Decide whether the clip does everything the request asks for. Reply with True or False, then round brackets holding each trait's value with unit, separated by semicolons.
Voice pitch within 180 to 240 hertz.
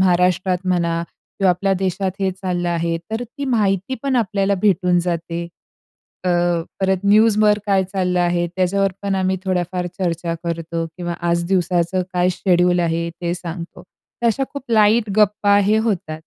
True (185 Hz)